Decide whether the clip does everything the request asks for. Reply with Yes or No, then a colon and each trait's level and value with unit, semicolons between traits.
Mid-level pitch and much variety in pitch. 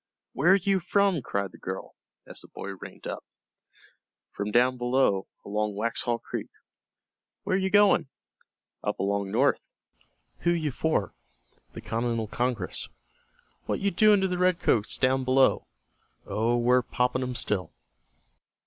No: low, 125 Hz; wide, 8.1 semitones